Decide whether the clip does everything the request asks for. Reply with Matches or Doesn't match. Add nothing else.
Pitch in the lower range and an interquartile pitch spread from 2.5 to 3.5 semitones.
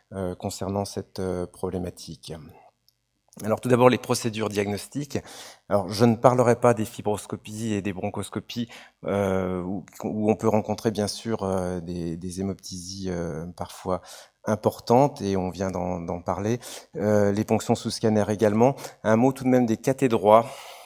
Matches